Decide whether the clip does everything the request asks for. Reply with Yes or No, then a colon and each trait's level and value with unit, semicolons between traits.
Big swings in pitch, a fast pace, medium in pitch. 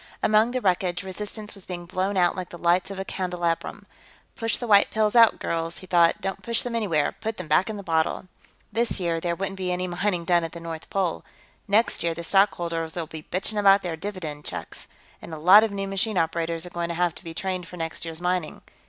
No: average, 3.0 semitones; fast, 230 wpm; medium, 180 Hz